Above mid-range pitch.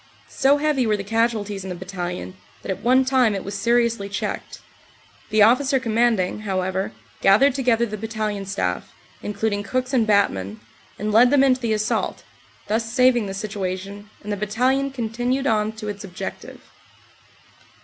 Yes: high, 215 Hz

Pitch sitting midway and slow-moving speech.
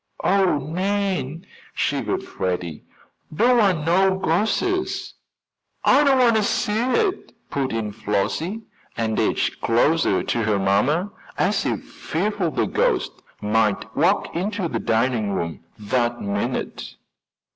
Yes: medium, 160 Hz; slow, 125 wpm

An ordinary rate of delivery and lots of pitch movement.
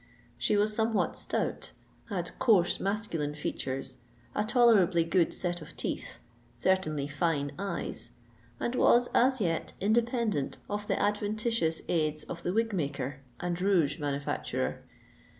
No: slow, 130 wpm; wide, 5.8 semitones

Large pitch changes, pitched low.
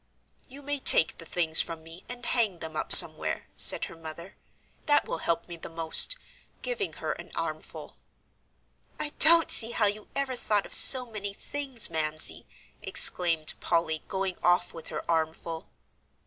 No: wide, 7.0 semitones; medium, 180 Hz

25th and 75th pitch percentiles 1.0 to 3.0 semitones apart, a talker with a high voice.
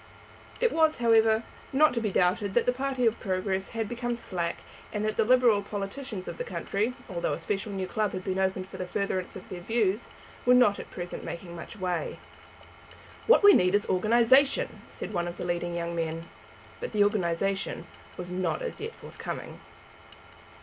No: average, 4.5 semitones; high, 205 Hz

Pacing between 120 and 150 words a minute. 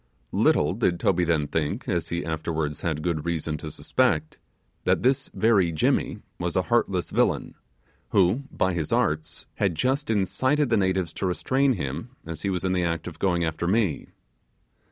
No: average, 175 wpm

